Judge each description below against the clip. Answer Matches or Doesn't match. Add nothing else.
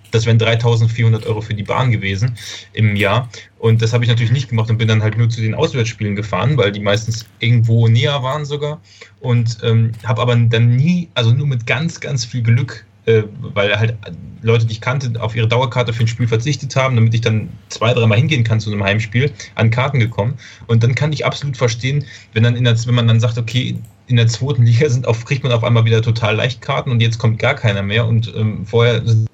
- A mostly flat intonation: Matches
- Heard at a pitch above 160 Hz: Doesn't match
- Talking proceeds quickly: Matches